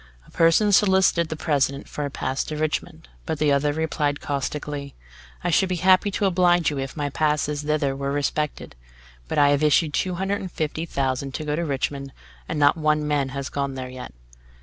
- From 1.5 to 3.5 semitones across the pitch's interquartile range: Yes, average, 2.8 semitones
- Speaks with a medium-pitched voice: Yes, medium, 150 Hz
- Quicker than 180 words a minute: Yes, average, 200 wpm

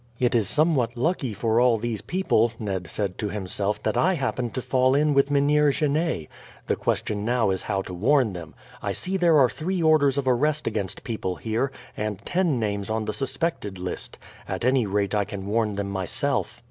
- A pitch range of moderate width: No, wide, 5.8 semitones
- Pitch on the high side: No, low, 120 Hz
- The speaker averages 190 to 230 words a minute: Yes, average, 200 wpm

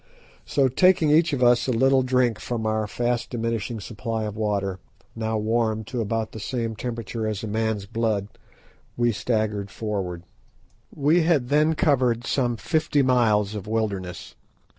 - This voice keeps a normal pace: Yes, average, 155 wpm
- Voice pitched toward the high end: No, low, 115 Hz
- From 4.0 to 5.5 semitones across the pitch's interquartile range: No, average, 2.9 semitones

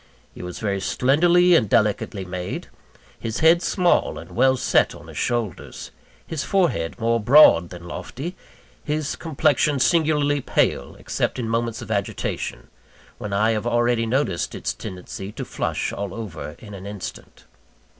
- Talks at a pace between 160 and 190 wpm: No, average, 150 wpm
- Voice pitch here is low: Yes, low, 115 Hz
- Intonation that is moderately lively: No, wide, 6.5 semitones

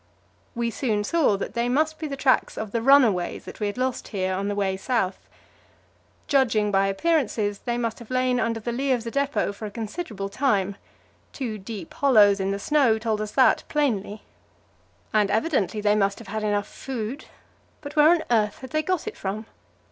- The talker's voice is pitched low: No, high, 225 Hz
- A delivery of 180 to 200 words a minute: Yes, average, 195 wpm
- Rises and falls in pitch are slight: No, average, 4.6 semitones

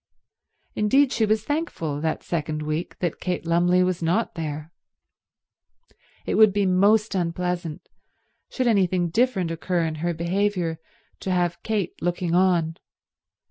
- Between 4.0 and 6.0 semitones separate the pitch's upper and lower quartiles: No, average, 3.5 semitones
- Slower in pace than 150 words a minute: Yes, slow, 135 wpm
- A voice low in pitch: No, medium, 180 Hz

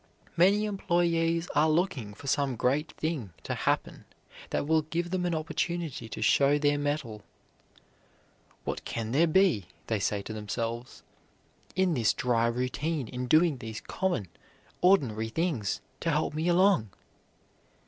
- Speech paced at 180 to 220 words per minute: No, average, 140 wpm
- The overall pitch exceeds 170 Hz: No, medium, 150 Hz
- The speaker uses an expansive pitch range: Yes, wide, 6.6 semitones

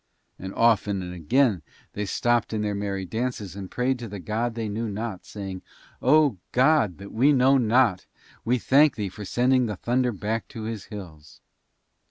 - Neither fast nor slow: Yes, average, 180 wpm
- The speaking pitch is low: Yes, low, 110 Hz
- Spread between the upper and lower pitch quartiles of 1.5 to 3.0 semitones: No, average, 3.9 semitones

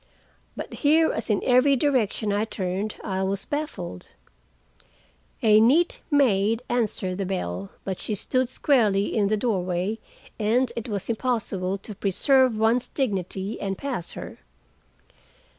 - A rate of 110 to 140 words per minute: Yes, slow, 135 wpm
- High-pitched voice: Yes, high, 215 Hz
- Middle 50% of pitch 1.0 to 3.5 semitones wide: No, average, 4.4 semitones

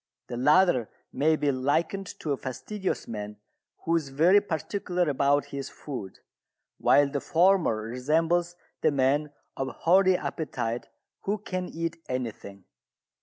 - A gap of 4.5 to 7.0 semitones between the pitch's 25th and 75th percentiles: Yes, average, 5.2 semitones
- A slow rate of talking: Yes, slow, 130 wpm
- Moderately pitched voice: Yes, medium, 150 Hz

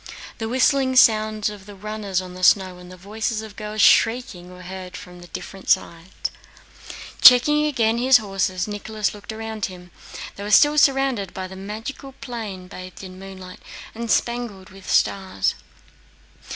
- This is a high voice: Yes, high, 205 Hz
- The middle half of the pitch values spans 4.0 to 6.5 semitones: No, average, 3.3 semitones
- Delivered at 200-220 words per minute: No, average, 155 wpm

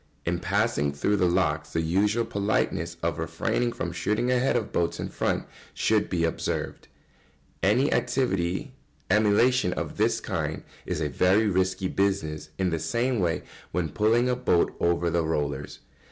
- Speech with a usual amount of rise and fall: Yes, average, 4.7 semitones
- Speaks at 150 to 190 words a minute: Yes, average, 160 wpm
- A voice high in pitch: No, very low, 95 Hz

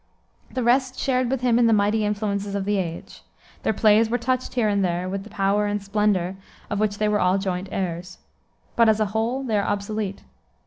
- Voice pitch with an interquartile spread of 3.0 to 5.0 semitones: No, narrow, 2.4 semitones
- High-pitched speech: Yes, high, 210 Hz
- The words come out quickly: Yes, fast, 215 wpm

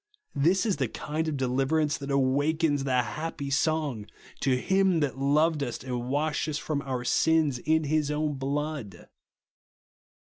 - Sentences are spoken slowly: No, average, 155 wpm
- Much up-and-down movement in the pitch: No, average, 2.8 semitones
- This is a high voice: No, medium, 145 Hz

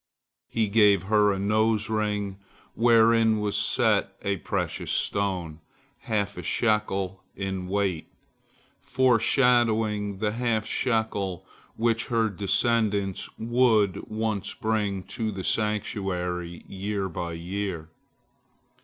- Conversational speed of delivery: No, slow, 105 wpm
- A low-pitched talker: Yes, low, 105 Hz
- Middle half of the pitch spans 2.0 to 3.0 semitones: Yes, narrow, 2.4 semitones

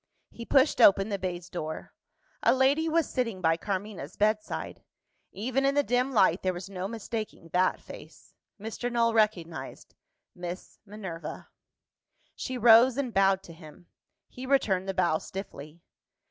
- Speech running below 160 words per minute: Yes, average, 145 wpm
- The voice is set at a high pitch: Yes, high, 200 Hz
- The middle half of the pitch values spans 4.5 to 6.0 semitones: Yes, average, 5.1 semitones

